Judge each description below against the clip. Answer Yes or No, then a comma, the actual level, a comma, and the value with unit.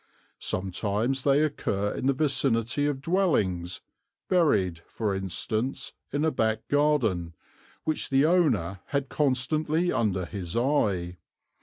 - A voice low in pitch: Yes, low, 125 Hz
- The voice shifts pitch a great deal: Yes, wide, 7.1 semitones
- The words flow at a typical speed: No, slow, 120 wpm